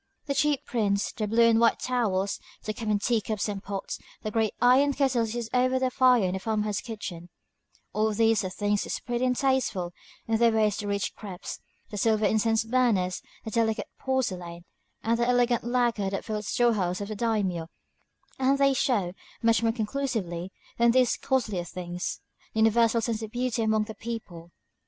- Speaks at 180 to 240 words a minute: Yes, average, 185 wpm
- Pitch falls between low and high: No, high, 220 Hz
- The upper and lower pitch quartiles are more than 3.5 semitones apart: No, average, 3.1 semitones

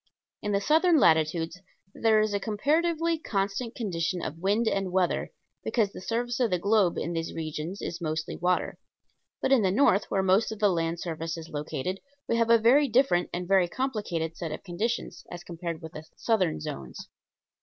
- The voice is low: No, high, 190 Hz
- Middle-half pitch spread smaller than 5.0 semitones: No, average, 5.3 semitones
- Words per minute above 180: Yes, average, 190 wpm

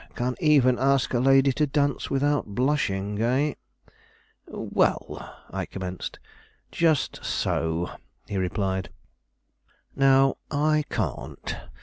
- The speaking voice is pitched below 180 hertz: Yes, low, 135 Hz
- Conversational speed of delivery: No, slow, 105 wpm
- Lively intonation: Yes, wide, 5.9 semitones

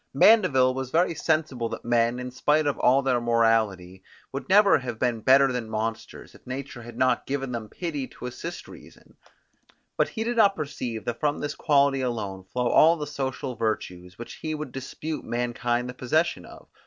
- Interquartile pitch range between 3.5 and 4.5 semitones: Yes, average, 3.9 semitones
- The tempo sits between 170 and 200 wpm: Yes, average, 185 wpm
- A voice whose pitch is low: Yes, low, 130 Hz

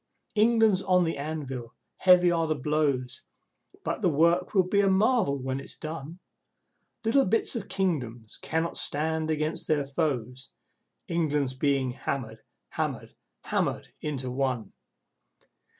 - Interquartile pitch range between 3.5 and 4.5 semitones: No, average, 5.2 semitones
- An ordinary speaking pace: No, slow, 130 wpm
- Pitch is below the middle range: No, medium, 155 Hz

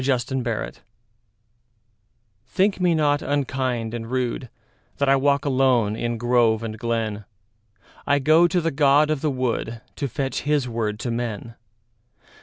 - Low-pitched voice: Yes, low, 125 Hz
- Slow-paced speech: Yes, slow, 130 wpm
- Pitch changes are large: No, average, 3.7 semitones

